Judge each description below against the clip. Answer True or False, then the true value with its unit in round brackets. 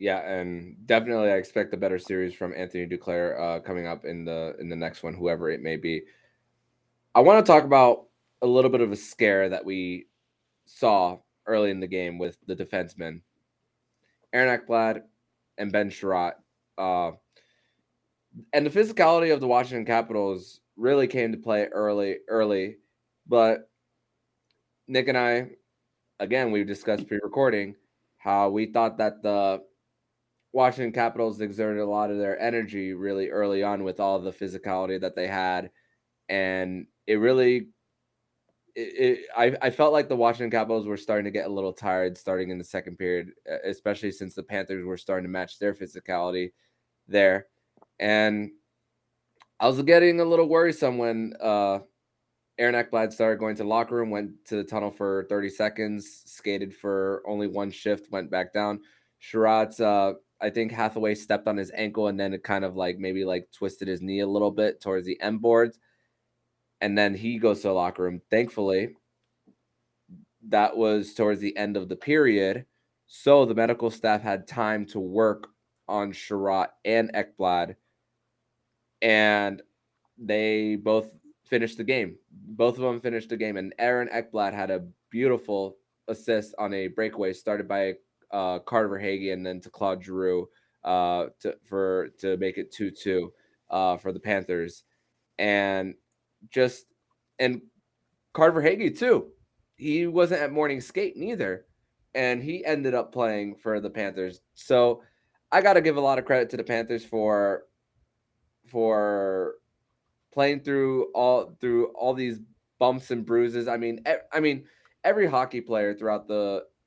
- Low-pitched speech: True (105 Hz)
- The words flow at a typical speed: True (165 wpm)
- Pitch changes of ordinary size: True (3.6 semitones)